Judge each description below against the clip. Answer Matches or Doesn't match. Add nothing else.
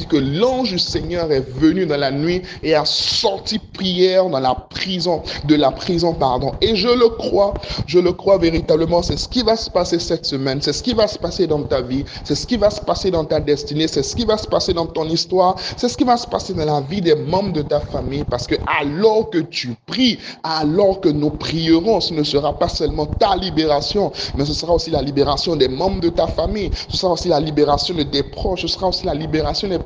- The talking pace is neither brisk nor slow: Doesn't match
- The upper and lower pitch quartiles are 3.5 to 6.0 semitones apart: Matches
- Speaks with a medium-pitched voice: Matches